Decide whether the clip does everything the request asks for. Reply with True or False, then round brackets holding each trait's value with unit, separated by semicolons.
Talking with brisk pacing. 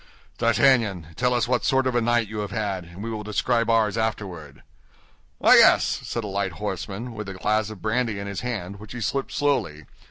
True (210 wpm)